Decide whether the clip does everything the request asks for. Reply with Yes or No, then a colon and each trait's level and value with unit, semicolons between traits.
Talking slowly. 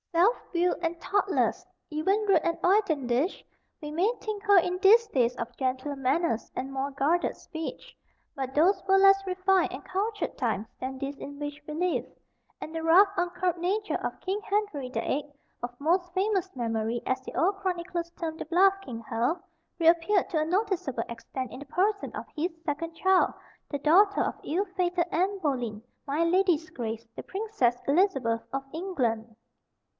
No: average, 170 wpm